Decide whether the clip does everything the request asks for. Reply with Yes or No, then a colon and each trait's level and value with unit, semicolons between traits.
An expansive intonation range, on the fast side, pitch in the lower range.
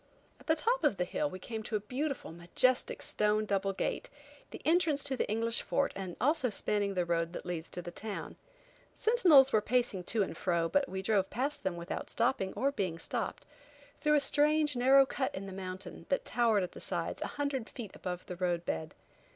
No: wide, 6.9 semitones; fast, 210 wpm; high, 215 Hz